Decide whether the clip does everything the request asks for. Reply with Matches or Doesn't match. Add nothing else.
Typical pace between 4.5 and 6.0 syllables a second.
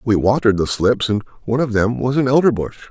Doesn't match